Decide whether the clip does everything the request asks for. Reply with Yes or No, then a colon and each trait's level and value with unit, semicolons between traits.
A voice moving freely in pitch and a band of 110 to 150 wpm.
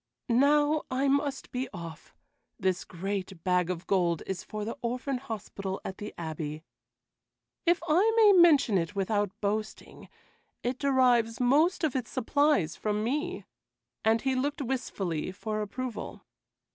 Yes: wide, 6.4 semitones; average, 140 wpm